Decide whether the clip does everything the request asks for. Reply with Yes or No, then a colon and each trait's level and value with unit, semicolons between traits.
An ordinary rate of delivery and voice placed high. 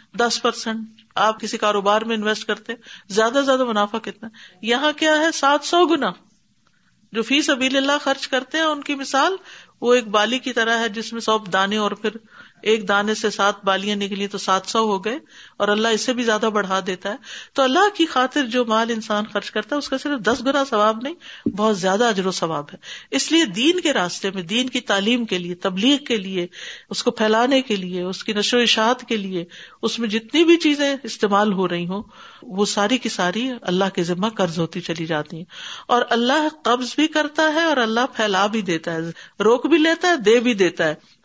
No: fast, 220 wpm; high, 225 Hz